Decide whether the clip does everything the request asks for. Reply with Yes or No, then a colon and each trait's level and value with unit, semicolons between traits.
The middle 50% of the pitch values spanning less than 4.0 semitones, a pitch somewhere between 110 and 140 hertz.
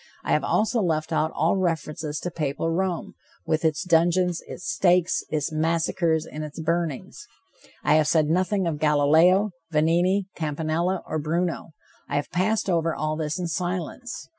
No: narrow, 2.6 semitones; medium, 165 Hz